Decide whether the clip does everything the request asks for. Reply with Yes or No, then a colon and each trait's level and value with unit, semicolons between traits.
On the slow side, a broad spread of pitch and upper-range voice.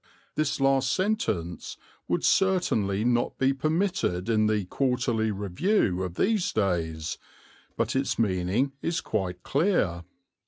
No: slow, 120 wpm; wide, 8.7 semitones; low, 115 Hz